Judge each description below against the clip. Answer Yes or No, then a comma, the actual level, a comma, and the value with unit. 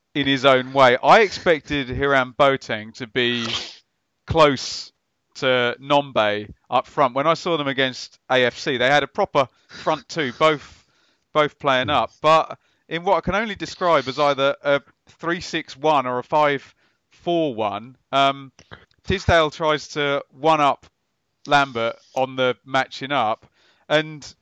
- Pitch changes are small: No, average, 3.5 semitones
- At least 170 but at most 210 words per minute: No, average, 145 wpm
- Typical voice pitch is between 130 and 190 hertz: Yes, medium, 140 Hz